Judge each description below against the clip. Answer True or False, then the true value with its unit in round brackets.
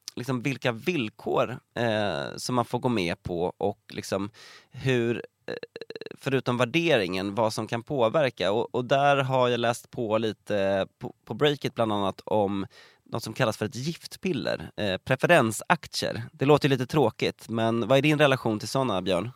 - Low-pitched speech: True (125 Hz)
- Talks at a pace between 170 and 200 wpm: True (175 wpm)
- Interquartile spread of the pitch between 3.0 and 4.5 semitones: True (4.0 semitones)